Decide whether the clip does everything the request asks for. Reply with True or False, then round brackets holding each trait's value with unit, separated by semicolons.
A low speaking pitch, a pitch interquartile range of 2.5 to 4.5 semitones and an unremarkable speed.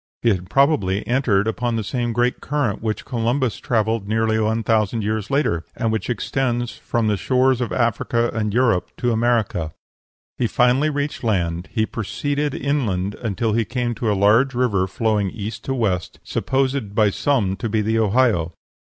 True (115 Hz; 3.2 semitones; 175 wpm)